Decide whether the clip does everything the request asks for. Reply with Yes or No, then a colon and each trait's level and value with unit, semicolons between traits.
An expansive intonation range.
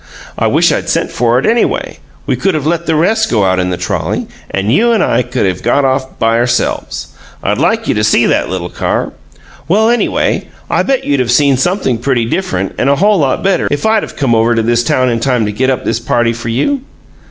Yes: wide, 6.5 semitones